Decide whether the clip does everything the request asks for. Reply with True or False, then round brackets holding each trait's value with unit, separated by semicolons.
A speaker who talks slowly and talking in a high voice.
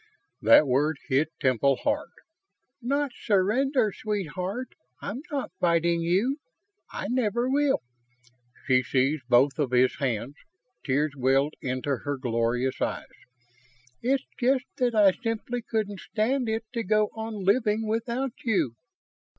True (125 wpm; 200 Hz)